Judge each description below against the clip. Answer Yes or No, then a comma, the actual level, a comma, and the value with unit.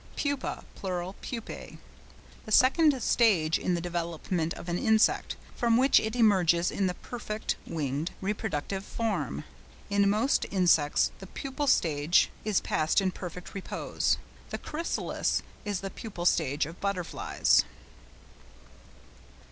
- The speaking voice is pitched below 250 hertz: Yes, high, 190 Hz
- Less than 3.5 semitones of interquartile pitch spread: No, average, 4.5 semitones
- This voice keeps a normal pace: No, slow, 125 wpm